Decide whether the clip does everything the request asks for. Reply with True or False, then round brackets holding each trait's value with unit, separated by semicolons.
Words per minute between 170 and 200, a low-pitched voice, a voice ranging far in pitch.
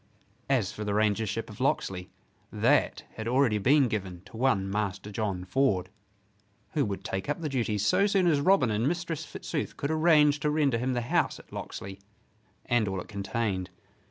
True (180 wpm; 115 Hz; 6.1 semitones)